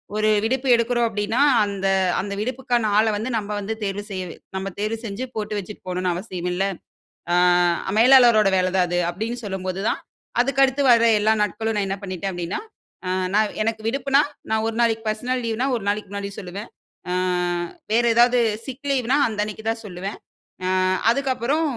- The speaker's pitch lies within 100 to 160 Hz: No, high, 220 Hz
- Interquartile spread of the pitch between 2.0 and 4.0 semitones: Yes, average, 3.4 semitones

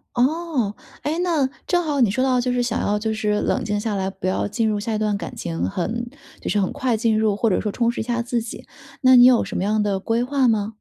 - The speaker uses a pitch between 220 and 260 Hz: Yes, high, 225 Hz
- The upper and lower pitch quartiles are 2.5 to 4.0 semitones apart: Yes, average, 3.2 semitones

